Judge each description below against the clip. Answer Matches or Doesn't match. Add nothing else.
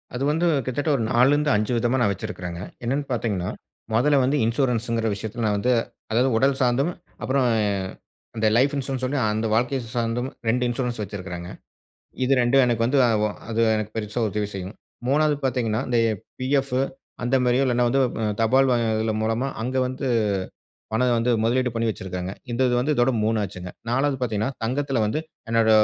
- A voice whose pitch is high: Doesn't match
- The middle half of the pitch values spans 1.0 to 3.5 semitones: Matches